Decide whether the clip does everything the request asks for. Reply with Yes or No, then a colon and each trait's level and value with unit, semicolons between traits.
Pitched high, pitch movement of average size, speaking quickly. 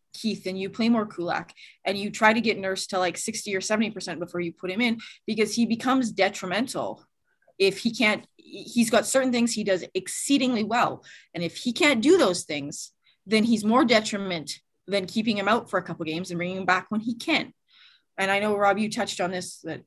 Yes: high, 210 Hz; average, 3.8 semitones; fast, 225 wpm